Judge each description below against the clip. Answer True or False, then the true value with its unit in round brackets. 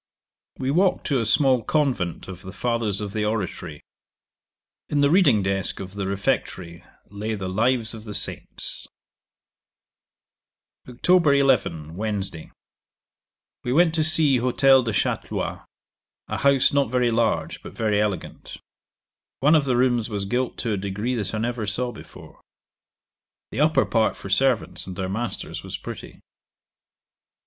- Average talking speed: True (145 wpm)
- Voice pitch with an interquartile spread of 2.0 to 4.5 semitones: False (4.9 semitones)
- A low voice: True (115 Hz)